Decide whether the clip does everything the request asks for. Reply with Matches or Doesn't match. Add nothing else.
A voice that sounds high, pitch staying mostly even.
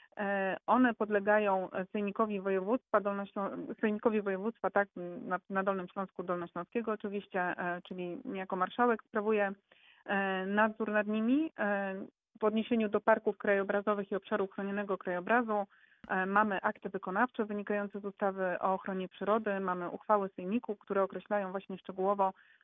Matches